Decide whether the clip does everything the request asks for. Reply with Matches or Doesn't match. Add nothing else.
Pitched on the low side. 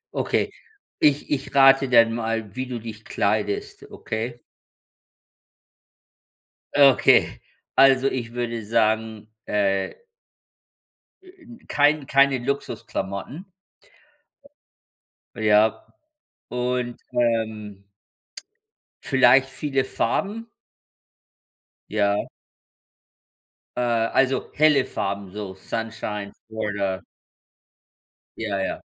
Matches